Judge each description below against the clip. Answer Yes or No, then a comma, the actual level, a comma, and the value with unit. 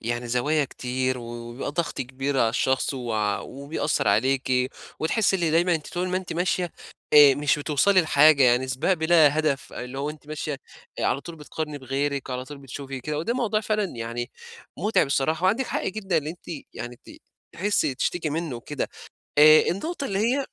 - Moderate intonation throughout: Yes, average, 4.6 semitones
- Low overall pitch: No, medium, 150 Hz